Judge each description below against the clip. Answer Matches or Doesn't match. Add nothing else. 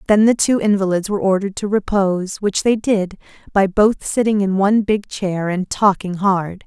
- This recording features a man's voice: Doesn't match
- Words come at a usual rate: Matches